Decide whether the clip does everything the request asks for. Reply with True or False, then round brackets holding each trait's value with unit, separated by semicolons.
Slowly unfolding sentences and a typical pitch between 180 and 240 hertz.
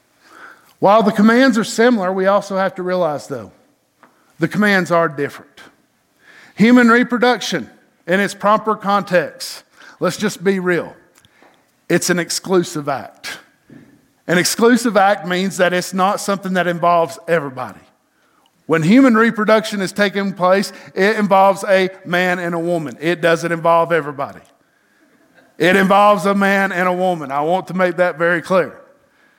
False (145 wpm; 185 Hz)